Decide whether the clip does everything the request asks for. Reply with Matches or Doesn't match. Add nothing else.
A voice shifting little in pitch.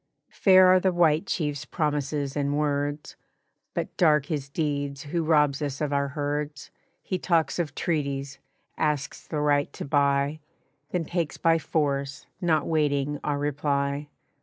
Matches